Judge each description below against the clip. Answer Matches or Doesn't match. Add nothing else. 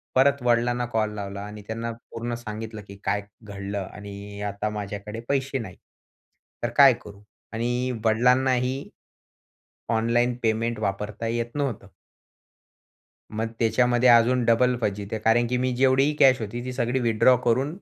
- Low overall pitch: Matches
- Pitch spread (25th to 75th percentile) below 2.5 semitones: Doesn't match